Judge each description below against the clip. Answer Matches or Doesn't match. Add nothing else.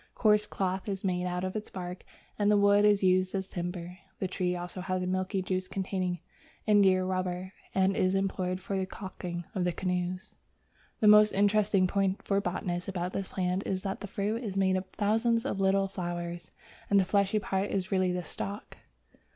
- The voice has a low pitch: Doesn't match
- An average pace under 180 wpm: Doesn't match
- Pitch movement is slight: Matches